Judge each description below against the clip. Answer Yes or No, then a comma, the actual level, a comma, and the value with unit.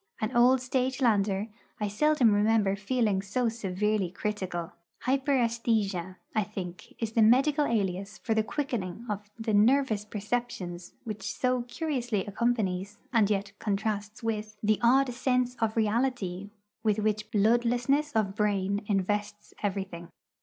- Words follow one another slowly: Yes, slow, 130 wpm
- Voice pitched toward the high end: Yes, high, 215 Hz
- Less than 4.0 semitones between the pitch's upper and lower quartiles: Yes, average, 3.2 semitones